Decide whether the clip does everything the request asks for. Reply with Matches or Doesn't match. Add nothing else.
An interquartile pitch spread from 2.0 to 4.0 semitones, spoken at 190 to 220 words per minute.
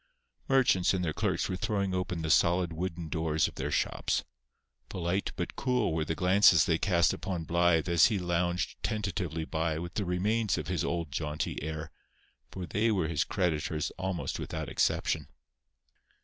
Doesn't match